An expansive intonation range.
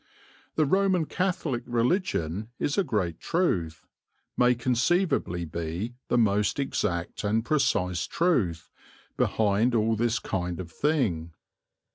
Yes: wide, 8.6 semitones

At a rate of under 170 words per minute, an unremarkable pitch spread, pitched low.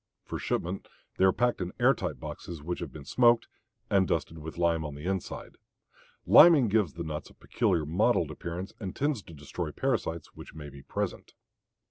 No: average, 185 wpm; average, 3.7 semitones; very low, 85 Hz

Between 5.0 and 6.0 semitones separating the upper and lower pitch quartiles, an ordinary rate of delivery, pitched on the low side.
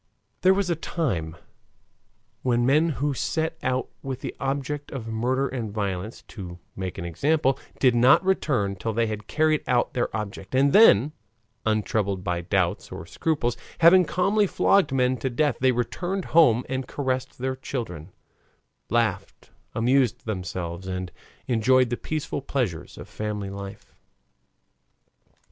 Yes: wide, 5.5 semitones; average, 145 wpm; low, 125 Hz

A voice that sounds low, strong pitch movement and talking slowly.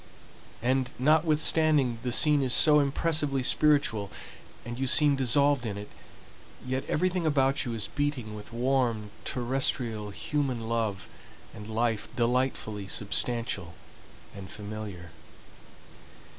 No: low, 125 Hz; average, 4.7 semitones; slow, 115 wpm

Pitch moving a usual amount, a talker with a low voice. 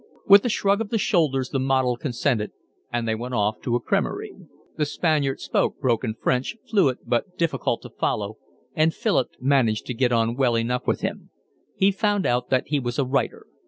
Yes: average, 4.6 semitones; low, 130 Hz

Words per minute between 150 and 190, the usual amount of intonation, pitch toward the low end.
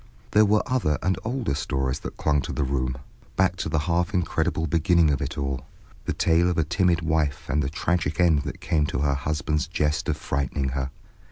No: fast, 205 wpm; average, 3.8 semitones; very low, 75 Hz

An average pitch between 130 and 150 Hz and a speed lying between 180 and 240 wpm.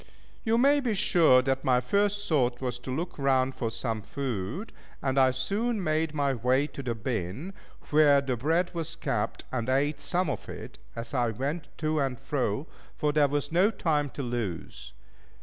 Yes: medium, 140 Hz; average, 185 wpm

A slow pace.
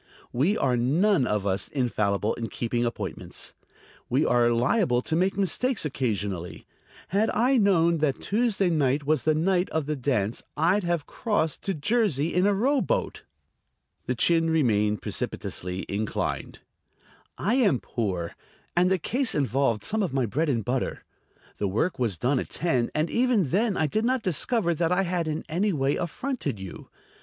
No: average, 165 wpm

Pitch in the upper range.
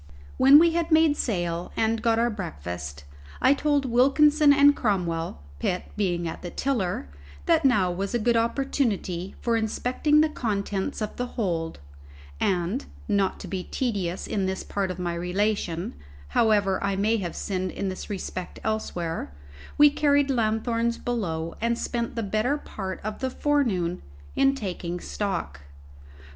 Yes: high, 210 Hz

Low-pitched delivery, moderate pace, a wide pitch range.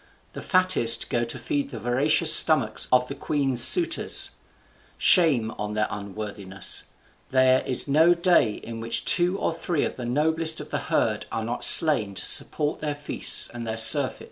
Yes: low, 130 Hz; average, 170 wpm; wide, 5.8 semitones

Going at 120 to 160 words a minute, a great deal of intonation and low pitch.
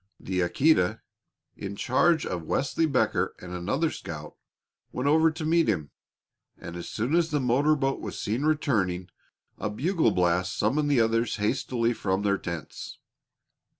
Yes: average, 150 wpm; wide, 8.4 semitones; low, 115 Hz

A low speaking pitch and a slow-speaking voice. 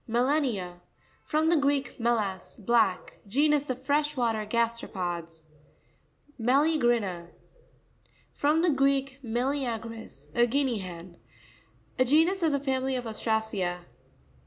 No: high, 240 Hz; slow, 110 wpm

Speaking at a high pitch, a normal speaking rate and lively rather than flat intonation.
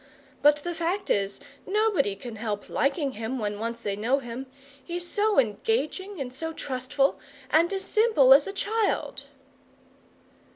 Yes: very high, 280 Hz; average, 150 wpm; wide, 8.2 semitones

